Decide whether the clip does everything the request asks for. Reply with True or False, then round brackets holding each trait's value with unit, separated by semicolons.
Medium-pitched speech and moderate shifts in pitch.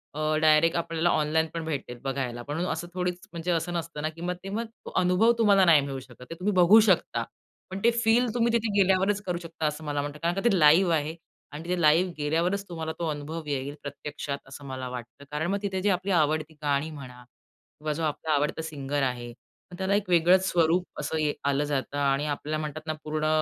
True (160 Hz; 3.6 semitones)